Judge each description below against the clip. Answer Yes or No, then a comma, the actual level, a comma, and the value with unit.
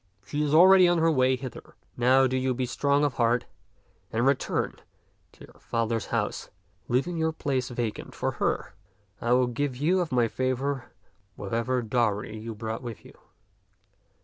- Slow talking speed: No, average, 165 wpm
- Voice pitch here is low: Yes, low, 130 Hz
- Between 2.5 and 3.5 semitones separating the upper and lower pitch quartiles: Yes, average, 3.2 semitones